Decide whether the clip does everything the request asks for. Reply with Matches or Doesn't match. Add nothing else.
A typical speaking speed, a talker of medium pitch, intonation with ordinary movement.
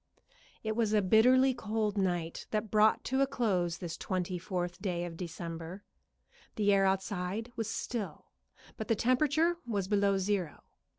Doesn't match